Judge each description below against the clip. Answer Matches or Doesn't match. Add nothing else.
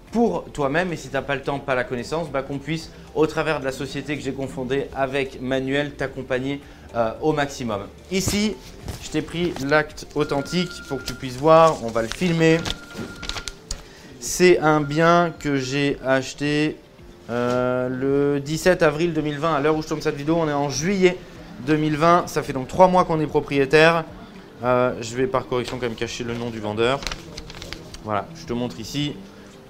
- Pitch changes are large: Doesn't match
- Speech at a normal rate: Matches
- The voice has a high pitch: Doesn't match